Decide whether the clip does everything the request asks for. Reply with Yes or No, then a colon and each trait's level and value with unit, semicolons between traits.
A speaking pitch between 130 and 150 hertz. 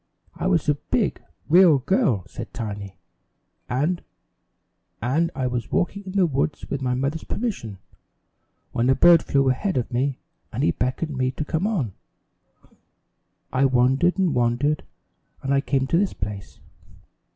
Yes: low, 135 Hz